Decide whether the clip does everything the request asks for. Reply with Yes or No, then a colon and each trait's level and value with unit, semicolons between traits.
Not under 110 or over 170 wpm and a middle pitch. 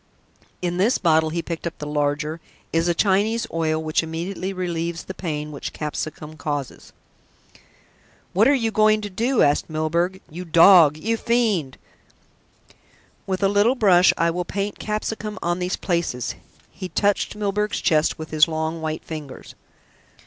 Yes: average, 155 wpm; medium, 175 Hz